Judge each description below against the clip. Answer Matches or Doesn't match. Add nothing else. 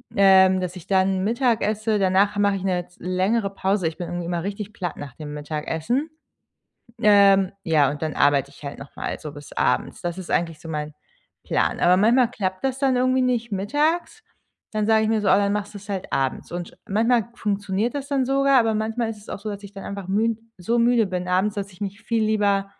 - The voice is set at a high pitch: Matches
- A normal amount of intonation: Matches